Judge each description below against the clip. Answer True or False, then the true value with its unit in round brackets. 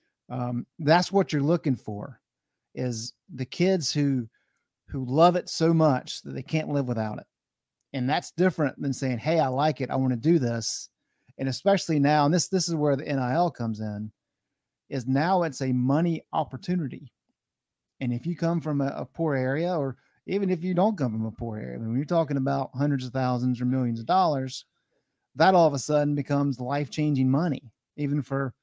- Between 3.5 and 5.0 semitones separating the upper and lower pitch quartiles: True (4.1 semitones)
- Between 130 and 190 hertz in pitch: True (140 Hz)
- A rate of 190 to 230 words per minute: True (200 wpm)